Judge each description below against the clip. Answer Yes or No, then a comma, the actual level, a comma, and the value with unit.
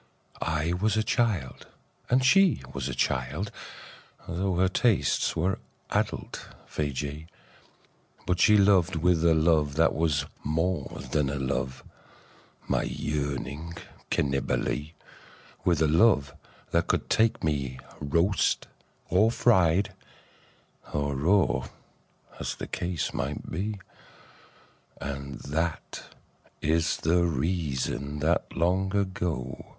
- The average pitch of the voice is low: Yes, very low, 80 Hz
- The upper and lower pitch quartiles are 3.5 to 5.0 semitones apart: Yes, average, 4.4 semitones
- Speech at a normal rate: No, slow, 115 wpm